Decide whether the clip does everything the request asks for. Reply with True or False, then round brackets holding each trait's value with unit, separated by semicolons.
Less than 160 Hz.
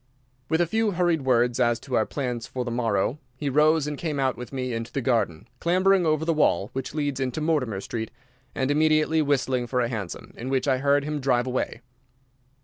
True (135 Hz)